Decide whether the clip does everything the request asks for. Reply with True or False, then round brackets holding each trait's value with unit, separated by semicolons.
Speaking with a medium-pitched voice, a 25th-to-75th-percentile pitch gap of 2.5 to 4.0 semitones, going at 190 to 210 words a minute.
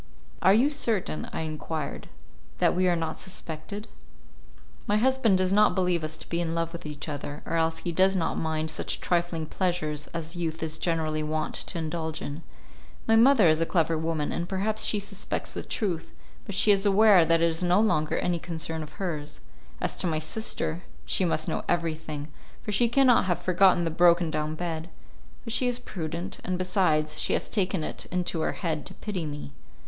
True (170 Hz; 3.2 semitones; 195 wpm)